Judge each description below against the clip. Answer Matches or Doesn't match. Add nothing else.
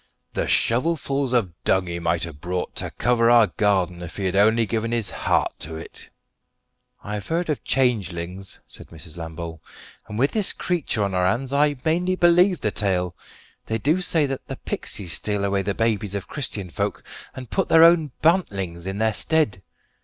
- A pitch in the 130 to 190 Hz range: Doesn't match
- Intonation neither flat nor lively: Doesn't match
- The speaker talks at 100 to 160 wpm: Doesn't match